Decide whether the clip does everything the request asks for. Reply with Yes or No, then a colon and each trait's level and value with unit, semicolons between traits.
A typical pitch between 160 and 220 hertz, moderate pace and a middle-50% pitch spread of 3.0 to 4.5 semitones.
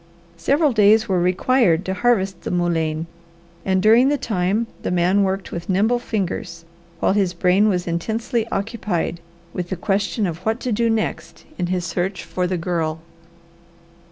Yes: high, 190 Hz; average, 160 wpm; average, 3.8 semitones